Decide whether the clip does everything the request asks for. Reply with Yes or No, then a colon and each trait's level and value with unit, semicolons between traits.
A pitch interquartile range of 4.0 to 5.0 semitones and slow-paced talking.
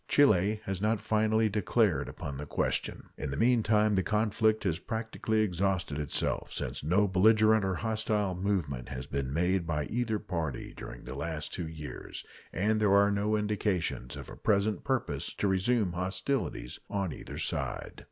No: average, 4.4 semitones; average, 160 wpm